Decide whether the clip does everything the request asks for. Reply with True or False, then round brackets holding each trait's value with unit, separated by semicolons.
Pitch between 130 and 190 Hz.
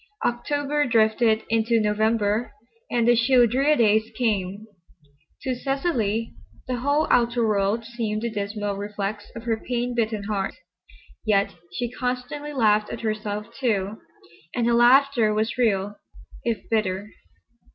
False (225 Hz)